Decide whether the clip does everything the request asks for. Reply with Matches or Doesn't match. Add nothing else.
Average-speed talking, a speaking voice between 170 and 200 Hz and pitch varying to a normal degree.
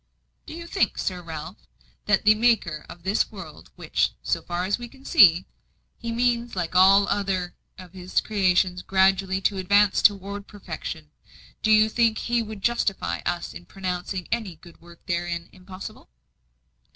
Matches